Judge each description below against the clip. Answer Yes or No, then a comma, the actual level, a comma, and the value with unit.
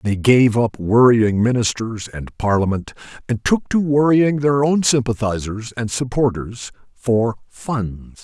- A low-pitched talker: Yes, low, 120 Hz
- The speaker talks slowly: Yes, slow, 125 wpm